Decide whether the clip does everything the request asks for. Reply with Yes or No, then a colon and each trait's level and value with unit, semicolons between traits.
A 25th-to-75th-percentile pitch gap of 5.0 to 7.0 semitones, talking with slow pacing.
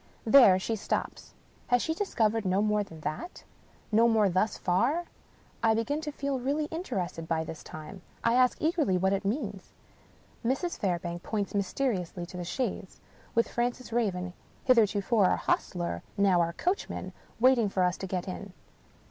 No: wide, 5.4 semitones; average, 165 wpm